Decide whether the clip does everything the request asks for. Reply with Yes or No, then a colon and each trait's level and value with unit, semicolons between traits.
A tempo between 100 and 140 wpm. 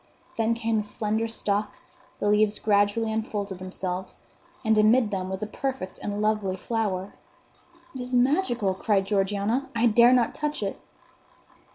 No: average, 150 wpm